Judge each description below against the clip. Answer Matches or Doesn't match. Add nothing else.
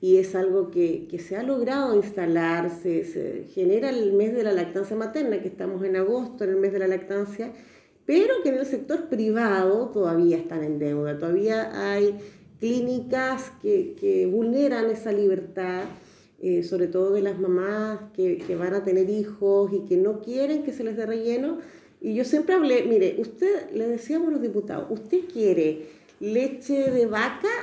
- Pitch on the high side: Matches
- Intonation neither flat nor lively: Doesn't match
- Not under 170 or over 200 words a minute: Matches